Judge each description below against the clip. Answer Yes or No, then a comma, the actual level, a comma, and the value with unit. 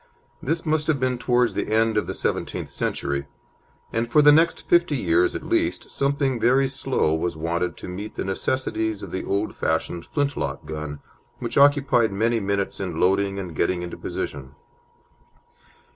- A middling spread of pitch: No, wide, 7.4 semitones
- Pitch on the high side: No, low, 110 Hz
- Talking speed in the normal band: Yes, average, 165 wpm